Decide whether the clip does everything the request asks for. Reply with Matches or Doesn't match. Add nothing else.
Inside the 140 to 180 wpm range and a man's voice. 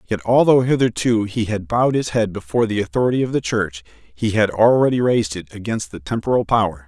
Doesn't match